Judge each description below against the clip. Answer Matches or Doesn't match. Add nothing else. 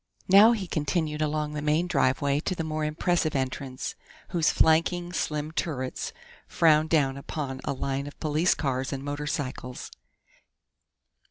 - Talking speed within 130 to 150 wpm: Matches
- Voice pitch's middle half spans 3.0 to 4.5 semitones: Doesn't match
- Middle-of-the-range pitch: Matches